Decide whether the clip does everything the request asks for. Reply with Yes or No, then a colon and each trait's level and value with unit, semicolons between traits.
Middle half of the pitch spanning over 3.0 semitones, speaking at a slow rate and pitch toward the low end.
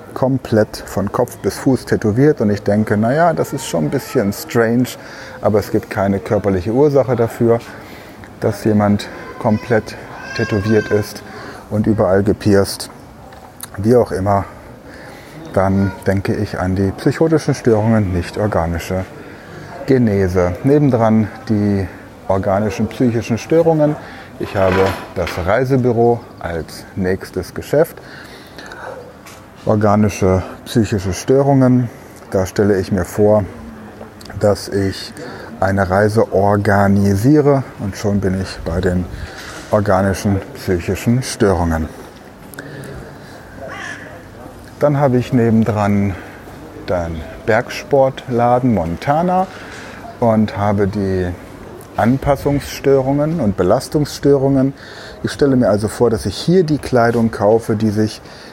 Yes: average, 4.0 semitones; slow, 110 wpm; low, 105 Hz